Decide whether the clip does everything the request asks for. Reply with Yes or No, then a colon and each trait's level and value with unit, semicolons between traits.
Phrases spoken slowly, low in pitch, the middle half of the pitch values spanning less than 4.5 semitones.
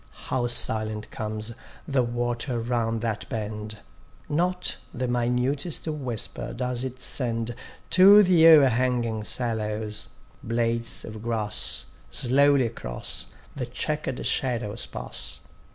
Yes: slow, 105 wpm; low, 120 Hz; average, 2.9 semitones